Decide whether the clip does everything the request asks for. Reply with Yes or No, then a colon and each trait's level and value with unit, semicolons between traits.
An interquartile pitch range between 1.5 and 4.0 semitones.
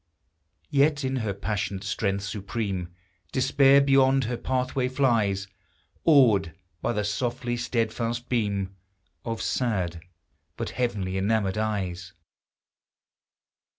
No: average, 4.5 semitones